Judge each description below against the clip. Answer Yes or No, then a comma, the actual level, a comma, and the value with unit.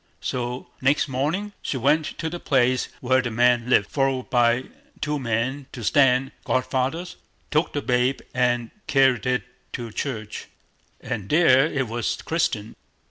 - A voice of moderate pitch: No, low, 130 Hz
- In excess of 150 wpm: No, average, 145 wpm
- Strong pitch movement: No, average, 2.8 semitones